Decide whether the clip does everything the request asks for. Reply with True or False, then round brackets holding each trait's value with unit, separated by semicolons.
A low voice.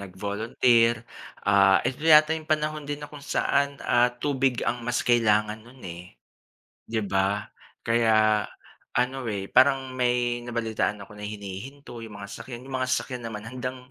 True (120 Hz)